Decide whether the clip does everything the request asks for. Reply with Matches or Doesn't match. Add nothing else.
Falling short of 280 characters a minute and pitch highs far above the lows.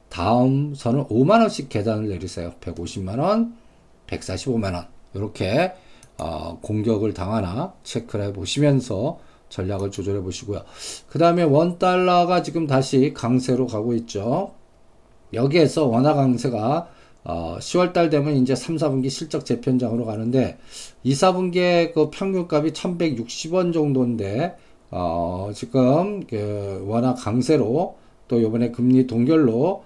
Matches